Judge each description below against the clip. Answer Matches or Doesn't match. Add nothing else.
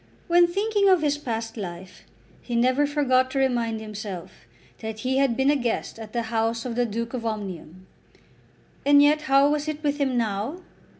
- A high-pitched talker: Matches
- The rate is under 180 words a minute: Doesn't match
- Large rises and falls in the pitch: Doesn't match